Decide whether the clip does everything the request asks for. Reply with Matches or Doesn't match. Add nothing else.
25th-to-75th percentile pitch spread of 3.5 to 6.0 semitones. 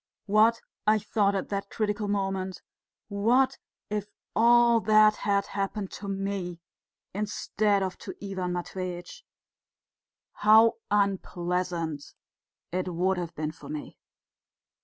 Doesn't match